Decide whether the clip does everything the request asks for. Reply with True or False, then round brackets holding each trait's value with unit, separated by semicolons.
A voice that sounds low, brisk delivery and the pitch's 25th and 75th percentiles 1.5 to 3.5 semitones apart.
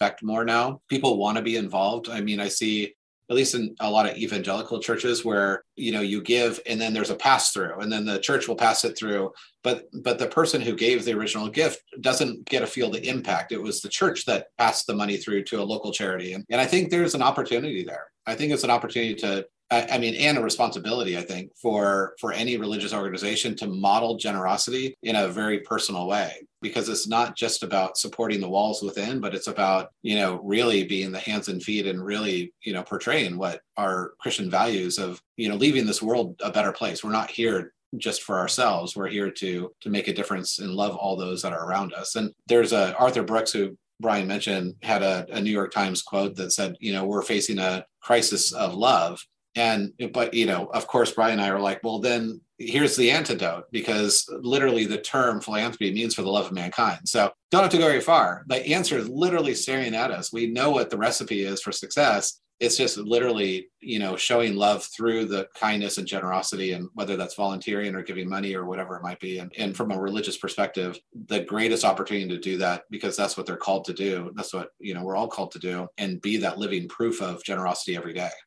True (105 Hz; 225 wpm; 3.0 semitones)